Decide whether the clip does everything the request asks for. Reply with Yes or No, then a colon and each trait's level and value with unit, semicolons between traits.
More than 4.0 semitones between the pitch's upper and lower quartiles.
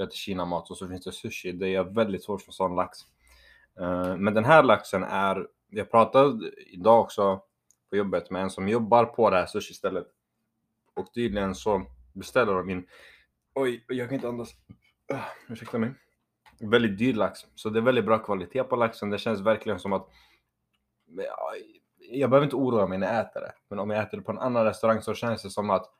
No: average, 3.6 semitones